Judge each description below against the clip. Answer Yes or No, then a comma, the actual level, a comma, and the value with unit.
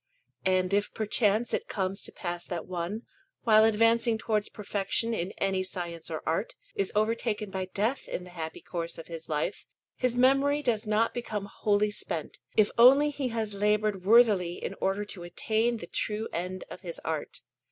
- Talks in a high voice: Yes, high, 205 Hz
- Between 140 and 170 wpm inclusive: No, average, 180 wpm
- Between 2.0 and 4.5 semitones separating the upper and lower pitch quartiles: Yes, average, 3.7 semitones